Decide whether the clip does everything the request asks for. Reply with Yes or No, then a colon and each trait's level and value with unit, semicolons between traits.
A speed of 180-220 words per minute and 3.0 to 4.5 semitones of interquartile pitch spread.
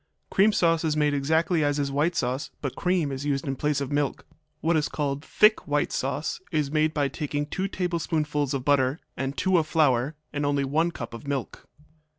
No: average, 200 wpm; narrow, 2.5 semitones